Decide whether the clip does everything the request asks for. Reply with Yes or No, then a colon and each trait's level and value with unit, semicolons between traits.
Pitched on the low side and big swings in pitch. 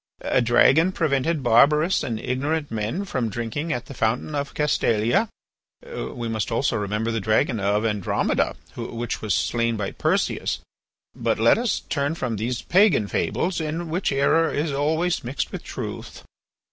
Yes: low, 130 Hz; wide, 5.8 semitones